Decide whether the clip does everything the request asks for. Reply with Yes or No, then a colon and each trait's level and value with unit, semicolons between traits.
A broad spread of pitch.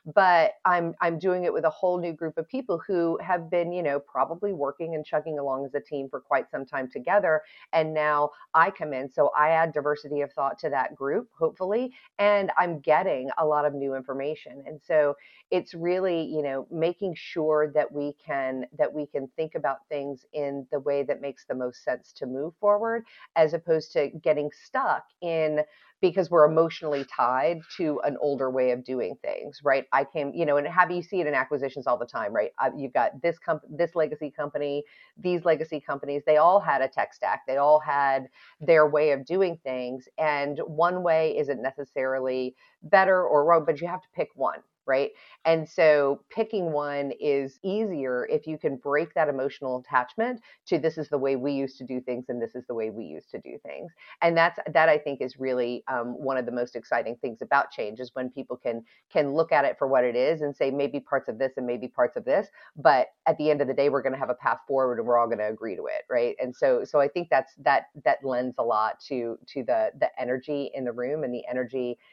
No: average, 3.6 semitones